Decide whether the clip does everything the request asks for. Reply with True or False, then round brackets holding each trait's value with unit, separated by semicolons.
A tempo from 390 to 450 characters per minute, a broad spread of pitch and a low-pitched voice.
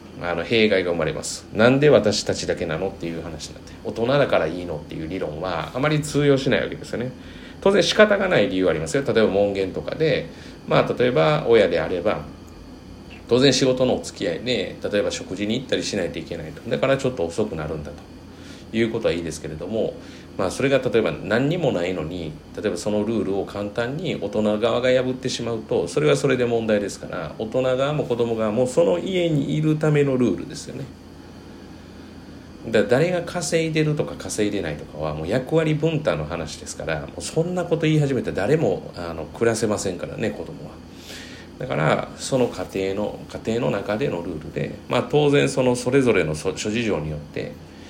True (395 characters per minute; 7.9 semitones; 110 Hz)